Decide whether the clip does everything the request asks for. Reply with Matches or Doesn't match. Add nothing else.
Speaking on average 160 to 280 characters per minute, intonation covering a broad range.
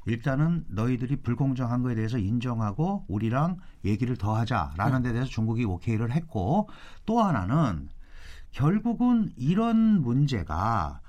Doesn't match